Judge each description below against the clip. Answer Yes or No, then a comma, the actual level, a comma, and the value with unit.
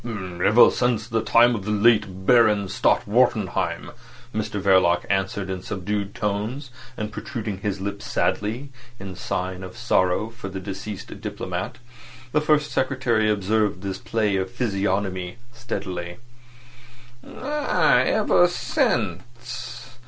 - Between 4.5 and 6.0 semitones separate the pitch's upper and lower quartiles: No, average, 3.8 semitones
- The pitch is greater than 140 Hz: No, low, 105 Hz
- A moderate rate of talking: No, slow, 125 wpm